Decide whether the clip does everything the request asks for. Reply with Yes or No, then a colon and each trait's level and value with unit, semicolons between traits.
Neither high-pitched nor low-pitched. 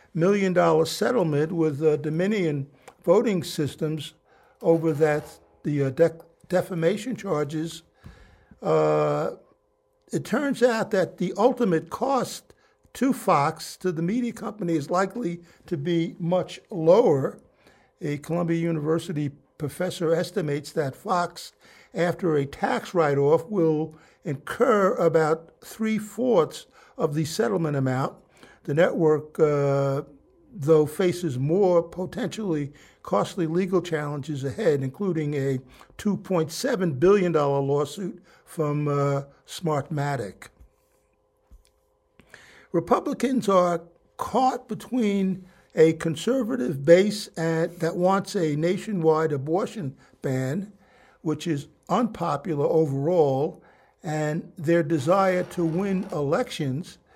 Yes: medium, 170 Hz